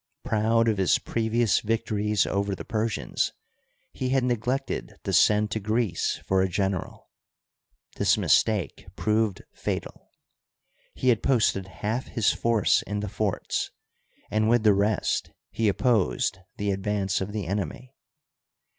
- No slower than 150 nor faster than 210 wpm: No, slow, 135 wpm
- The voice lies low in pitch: Yes, low, 105 Hz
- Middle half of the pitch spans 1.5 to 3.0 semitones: Yes, narrow, 2.5 semitones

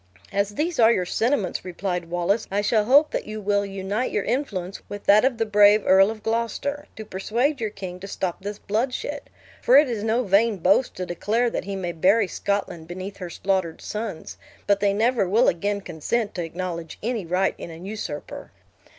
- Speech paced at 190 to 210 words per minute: Yes, average, 195 wpm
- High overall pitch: Yes, high, 205 Hz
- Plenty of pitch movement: No, average, 3.5 semitones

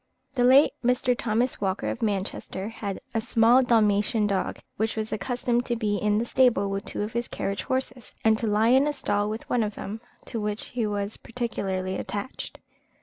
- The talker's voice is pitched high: Yes, high, 220 Hz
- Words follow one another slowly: No, average, 195 wpm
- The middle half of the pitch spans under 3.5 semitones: Yes, average, 2.9 semitones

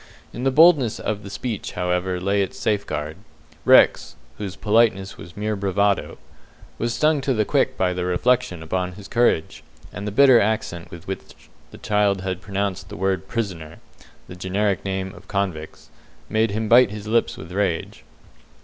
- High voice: No, low, 100 Hz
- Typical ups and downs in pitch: Yes, average, 3.1 semitones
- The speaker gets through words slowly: No, average, 165 wpm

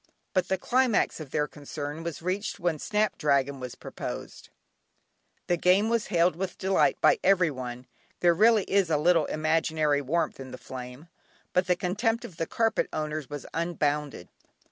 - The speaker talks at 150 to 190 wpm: Yes, average, 165 wpm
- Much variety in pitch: No, average, 4.5 semitones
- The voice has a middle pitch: Yes, medium, 165 Hz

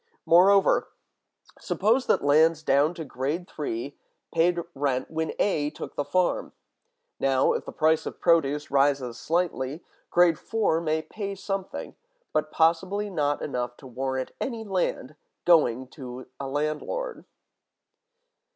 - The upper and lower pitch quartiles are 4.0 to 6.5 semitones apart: Yes, average, 4.5 semitones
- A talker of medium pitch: Yes, medium, 155 Hz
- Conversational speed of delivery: No, slow, 130 wpm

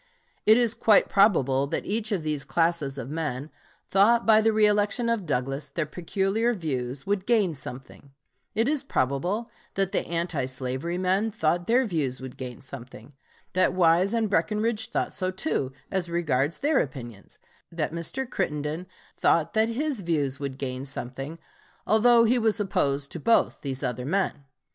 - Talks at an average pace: Yes, average, 160 wpm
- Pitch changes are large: Yes, wide, 7.6 semitones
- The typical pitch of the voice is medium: Yes, medium, 170 Hz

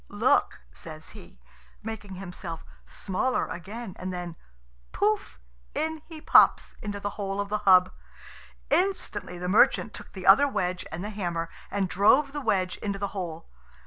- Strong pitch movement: No, average, 2.9 semitones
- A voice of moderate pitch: No, high, 200 Hz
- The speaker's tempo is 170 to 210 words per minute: No, average, 155 wpm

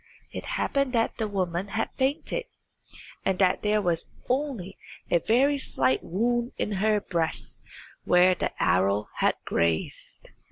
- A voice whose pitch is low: No, high, 200 Hz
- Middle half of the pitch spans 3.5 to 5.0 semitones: No, wide, 5.6 semitones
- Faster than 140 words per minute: No, slow, 135 wpm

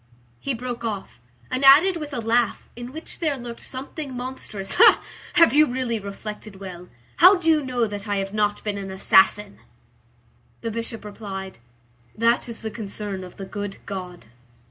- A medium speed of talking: Yes, average, 165 wpm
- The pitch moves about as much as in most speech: Yes, average, 4.3 semitones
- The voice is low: No, high, 225 Hz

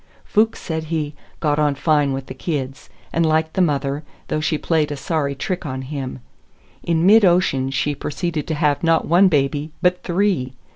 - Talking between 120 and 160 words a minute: No, average, 185 wpm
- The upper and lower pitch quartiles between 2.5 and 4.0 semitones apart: Yes, average, 3.3 semitones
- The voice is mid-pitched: Yes, medium, 155 Hz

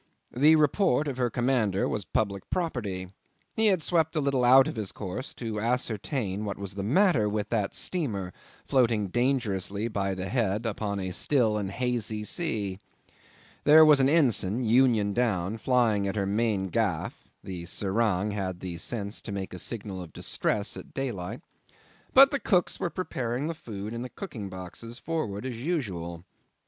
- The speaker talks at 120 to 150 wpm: No, average, 170 wpm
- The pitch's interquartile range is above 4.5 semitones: Yes, average, 5.0 semitones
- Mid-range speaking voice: No, low, 110 Hz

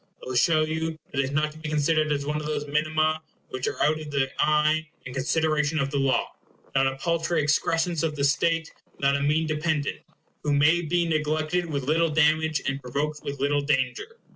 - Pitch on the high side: No, medium, 150 Hz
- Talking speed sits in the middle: No, fast, 210 wpm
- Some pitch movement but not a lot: No, narrow, 1.9 semitones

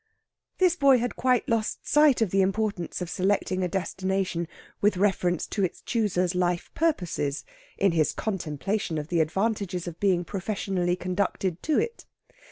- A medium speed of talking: Yes, average, 155 wpm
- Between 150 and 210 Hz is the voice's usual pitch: Yes, high, 190 Hz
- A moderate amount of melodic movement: Yes, average, 3.4 semitones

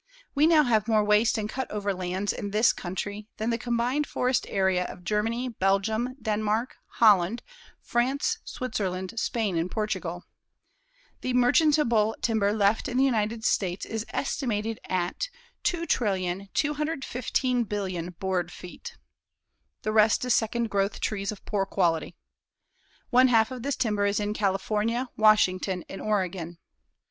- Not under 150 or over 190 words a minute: No, slow, 135 wpm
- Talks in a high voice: Yes, high, 215 Hz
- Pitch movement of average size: Yes, average, 3.9 semitones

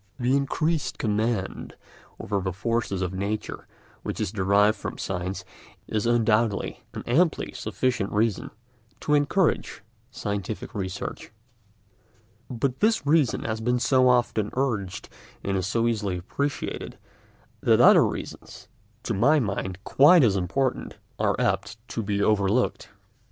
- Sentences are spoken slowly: Yes, slow, 130 wpm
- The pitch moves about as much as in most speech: Yes, average, 4.5 semitones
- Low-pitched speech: Yes, low, 110 Hz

